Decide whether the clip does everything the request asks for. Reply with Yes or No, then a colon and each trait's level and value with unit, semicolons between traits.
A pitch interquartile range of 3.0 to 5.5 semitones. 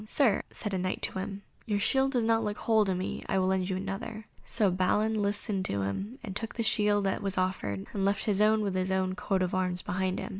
No: narrow, 2.4 semitones